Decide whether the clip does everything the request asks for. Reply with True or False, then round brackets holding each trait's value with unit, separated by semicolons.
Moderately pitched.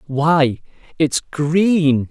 True (150 Hz)